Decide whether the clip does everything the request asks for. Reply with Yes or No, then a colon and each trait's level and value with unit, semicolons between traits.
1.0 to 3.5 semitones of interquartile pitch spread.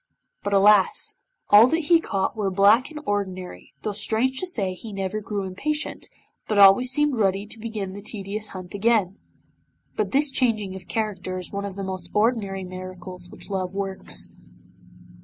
Yes: average, 2.9 semitones